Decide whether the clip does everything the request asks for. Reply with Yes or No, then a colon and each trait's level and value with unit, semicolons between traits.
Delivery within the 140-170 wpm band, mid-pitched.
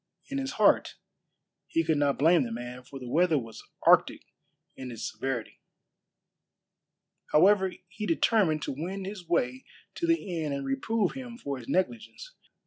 Yes: average, 155 wpm; medium, 165 Hz